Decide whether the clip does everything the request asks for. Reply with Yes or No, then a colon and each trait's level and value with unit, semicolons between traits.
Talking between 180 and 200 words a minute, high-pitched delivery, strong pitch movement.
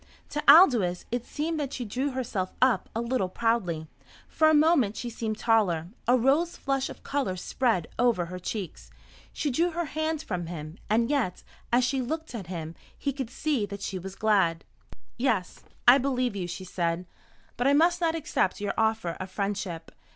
Yes: average, 185 wpm; high, 230 Hz; wide, 6.9 semitones